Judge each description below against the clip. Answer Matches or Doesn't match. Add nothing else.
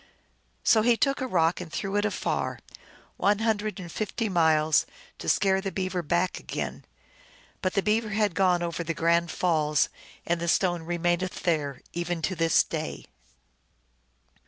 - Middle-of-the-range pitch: Matches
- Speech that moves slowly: Doesn't match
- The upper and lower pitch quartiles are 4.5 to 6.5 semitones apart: Doesn't match